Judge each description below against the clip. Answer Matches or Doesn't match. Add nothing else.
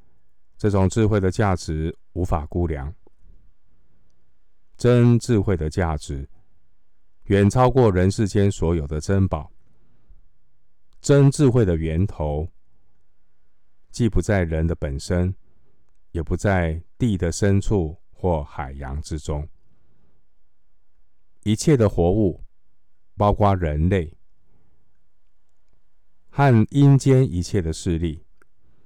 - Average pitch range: Matches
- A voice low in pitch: Matches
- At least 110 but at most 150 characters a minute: Matches